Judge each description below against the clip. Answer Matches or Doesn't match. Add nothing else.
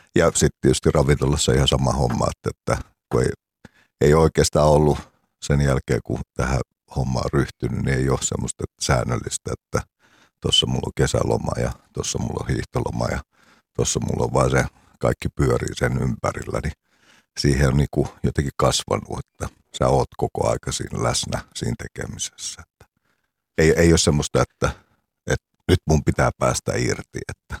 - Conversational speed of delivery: Doesn't match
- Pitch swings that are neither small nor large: Doesn't match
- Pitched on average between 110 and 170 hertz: Doesn't match